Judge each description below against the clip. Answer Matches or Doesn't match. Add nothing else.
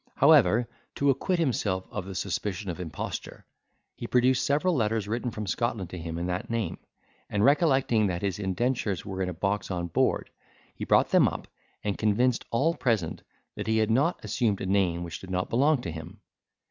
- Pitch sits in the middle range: Doesn't match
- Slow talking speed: Doesn't match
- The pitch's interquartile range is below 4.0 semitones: Doesn't match